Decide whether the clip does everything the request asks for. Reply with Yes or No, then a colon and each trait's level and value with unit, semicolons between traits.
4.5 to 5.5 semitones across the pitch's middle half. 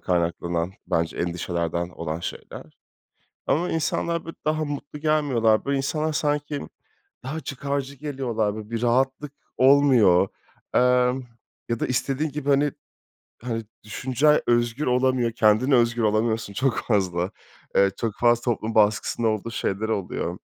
Yes: average, 4.8 semitones